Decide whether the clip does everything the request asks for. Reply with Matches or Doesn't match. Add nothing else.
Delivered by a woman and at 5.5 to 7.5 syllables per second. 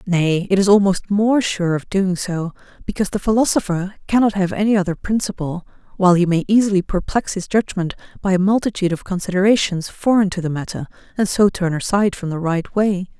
Matches